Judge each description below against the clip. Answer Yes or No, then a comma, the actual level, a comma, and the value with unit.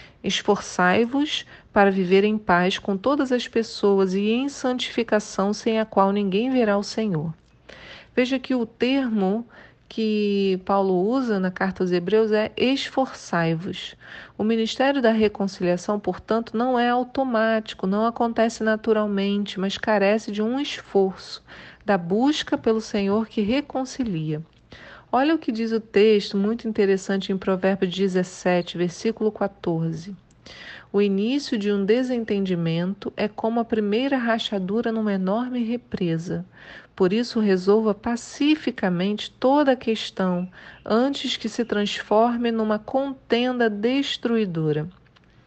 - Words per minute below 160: Yes, average, 125 wpm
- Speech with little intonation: No, average, 3.3 semitones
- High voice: Yes, high, 215 Hz